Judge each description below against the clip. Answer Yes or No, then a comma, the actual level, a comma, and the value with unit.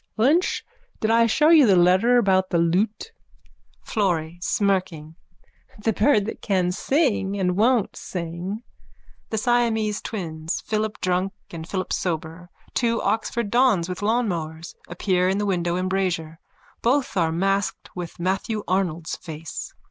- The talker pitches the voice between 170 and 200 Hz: Yes, high, 190 Hz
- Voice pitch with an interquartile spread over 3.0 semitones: Yes, average, 4.1 semitones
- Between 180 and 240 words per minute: No, slow, 135 wpm